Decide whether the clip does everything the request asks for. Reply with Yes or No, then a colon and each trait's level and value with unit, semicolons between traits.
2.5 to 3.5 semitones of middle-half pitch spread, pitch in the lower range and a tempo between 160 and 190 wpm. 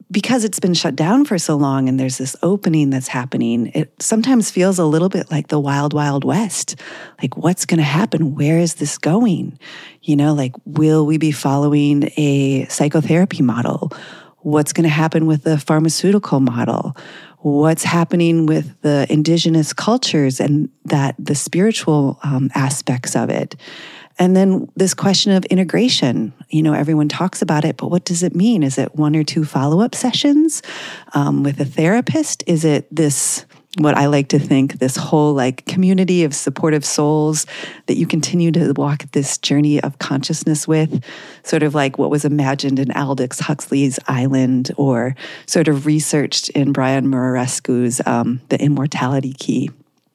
No: average, 3.2 semitones; medium, 150 Hz; average, 170 wpm